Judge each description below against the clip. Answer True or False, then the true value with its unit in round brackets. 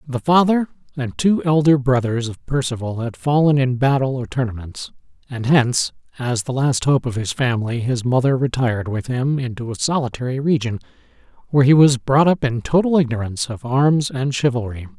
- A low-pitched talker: True (130 Hz)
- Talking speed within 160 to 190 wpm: True (175 wpm)